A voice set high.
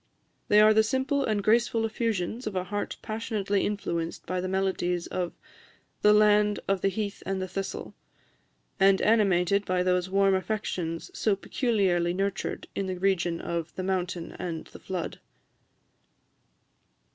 Yes: high, 195 Hz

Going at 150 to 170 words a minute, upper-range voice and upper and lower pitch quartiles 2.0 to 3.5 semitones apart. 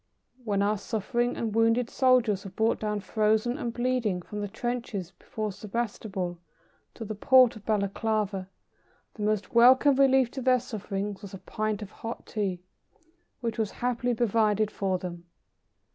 Yes: average, 155 wpm; high, 215 Hz; average, 3.1 semitones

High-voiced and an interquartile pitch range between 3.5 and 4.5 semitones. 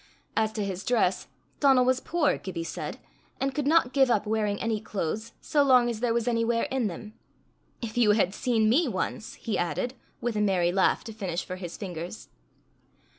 Yes: high, 220 Hz; average, 4.0 semitones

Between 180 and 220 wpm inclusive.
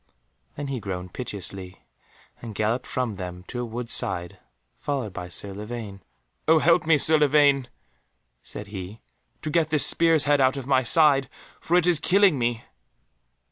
No: average, 165 wpm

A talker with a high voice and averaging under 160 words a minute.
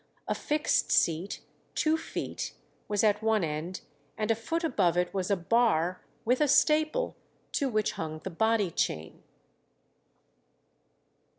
Yes: high, 210 Hz; slow, 135 wpm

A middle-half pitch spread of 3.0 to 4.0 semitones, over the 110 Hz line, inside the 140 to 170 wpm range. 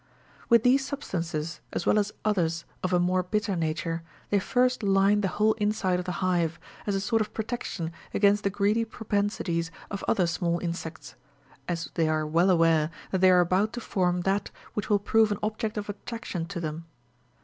No: average, 3.7 semitones; high, 190 Hz; average, 190 wpm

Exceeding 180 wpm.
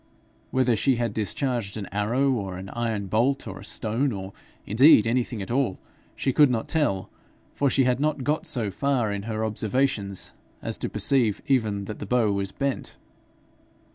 No: average, 175 wpm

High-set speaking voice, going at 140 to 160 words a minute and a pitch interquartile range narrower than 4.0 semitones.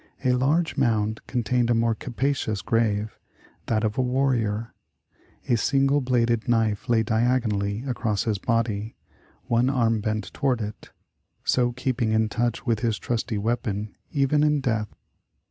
No: low, 115 Hz; average, 150 wpm; average, 2.7 semitones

